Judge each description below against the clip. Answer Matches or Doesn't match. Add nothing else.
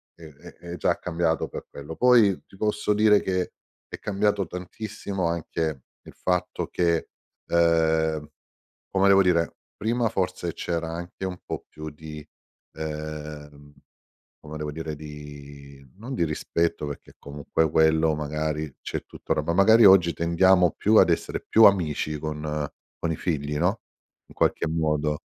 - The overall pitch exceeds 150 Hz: Doesn't match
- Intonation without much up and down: Doesn't match